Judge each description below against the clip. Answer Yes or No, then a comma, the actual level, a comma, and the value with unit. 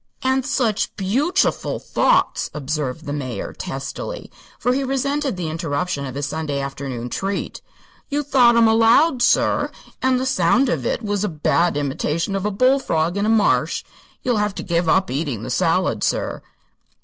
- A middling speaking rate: Yes, average, 165 wpm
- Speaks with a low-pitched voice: No, high, 195 Hz